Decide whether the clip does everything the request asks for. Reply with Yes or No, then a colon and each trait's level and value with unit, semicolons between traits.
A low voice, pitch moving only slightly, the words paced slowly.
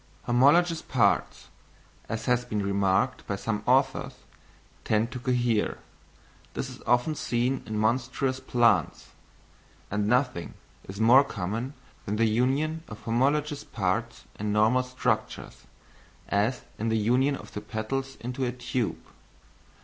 No: low, 120 Hz; average, 3.4 semitones; slow, 130 wpm